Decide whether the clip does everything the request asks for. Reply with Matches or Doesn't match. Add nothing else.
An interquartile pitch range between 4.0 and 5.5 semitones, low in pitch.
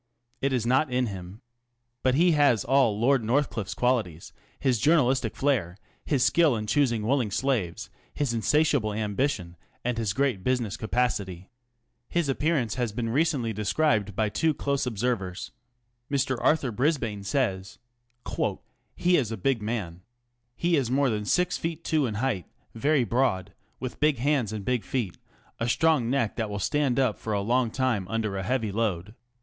Matches